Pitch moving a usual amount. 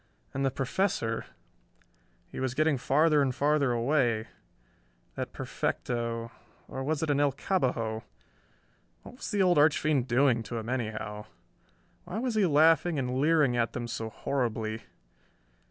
Yes: average, 4.6 semitones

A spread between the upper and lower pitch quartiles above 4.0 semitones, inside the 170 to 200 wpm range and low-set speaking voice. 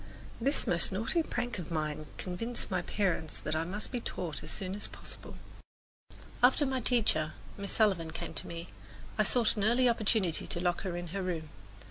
No: average, 5.2 semitones; average, 185 wpm; high, 190 Hz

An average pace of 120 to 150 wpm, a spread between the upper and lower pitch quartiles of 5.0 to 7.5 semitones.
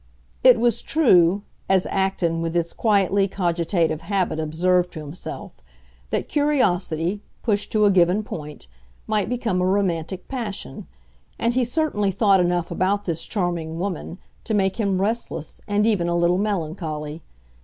No: average, 145 wpm; average, 3.5 semitones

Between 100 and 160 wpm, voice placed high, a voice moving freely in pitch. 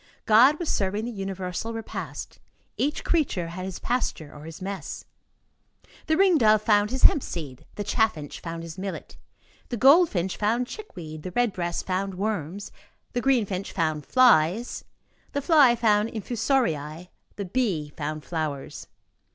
Yes: average, 150 wpm; high, 200 Hz; wide, 6.3 semitones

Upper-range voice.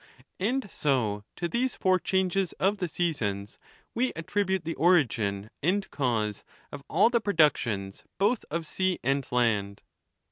No: medium, 165 Hz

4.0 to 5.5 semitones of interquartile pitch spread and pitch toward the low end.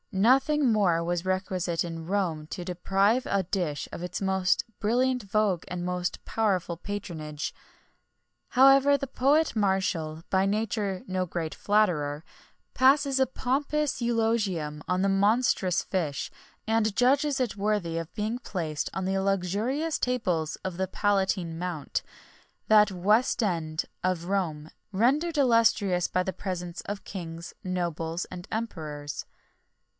No: average, 4.4 semitones; high, 190 Hz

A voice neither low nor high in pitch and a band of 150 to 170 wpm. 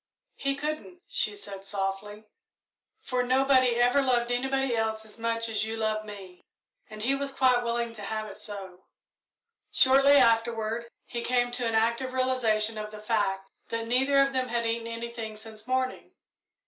No: high, 230 Hz; average, 165 wpm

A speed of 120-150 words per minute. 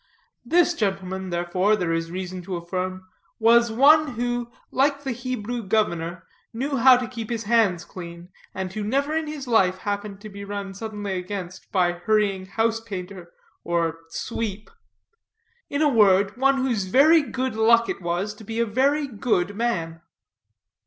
No: average, 160 wpm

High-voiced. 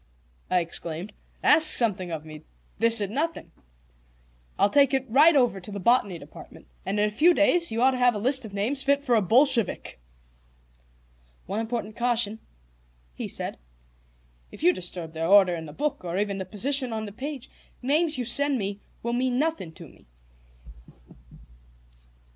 Yes: high, 225 Hz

